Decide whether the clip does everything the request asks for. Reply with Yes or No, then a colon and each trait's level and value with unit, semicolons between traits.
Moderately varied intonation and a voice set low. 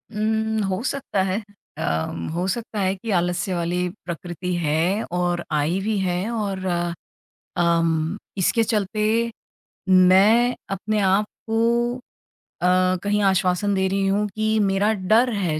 No: average, 3.1 semitones; high, 195 Hz